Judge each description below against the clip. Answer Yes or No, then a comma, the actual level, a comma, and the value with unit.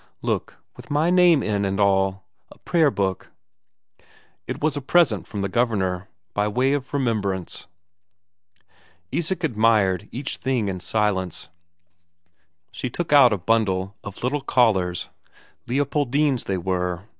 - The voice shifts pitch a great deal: Yes, wide, 6.3 semitones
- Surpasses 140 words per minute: No, slow, 135 wpm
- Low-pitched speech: Yes, low, 110 Hz